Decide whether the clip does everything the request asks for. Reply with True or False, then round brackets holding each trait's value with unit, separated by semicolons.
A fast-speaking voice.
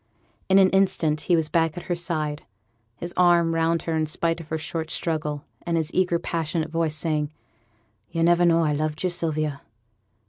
False (185 wpm)